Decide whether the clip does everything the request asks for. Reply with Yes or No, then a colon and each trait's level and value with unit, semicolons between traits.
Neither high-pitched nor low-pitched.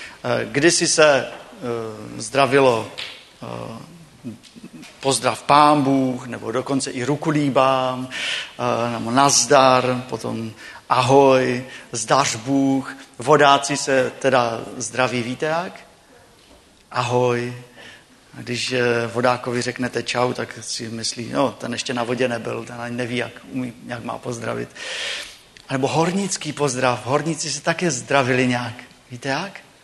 No: low, 125 Hz